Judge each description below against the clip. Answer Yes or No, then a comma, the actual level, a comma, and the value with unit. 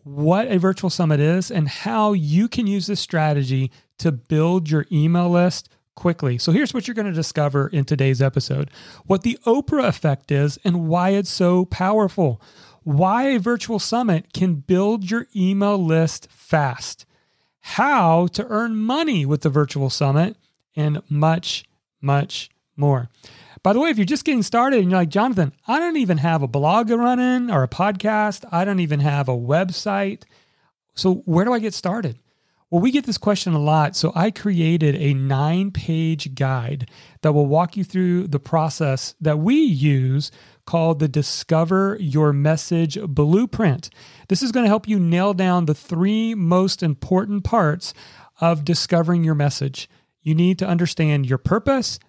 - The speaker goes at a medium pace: Yes, average, 170 wpm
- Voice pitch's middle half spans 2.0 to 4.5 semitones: No, average, 5.2 semitones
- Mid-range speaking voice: Yes, medium, 170 Hz